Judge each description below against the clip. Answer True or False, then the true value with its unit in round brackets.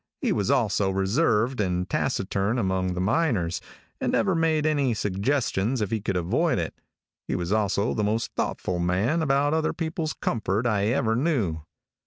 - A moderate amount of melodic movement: False (6.5 semitones)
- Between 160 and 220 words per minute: True (165 wpm)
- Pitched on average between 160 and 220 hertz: False (110 Hz)